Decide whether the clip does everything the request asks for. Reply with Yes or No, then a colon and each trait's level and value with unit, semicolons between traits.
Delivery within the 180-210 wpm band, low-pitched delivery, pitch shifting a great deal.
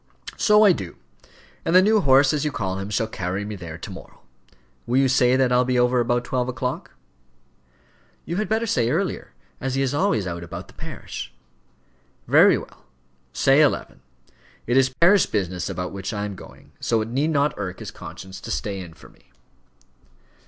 Yes: average, 190 wpm; low, 125 Hz; wide, 6.2 semitones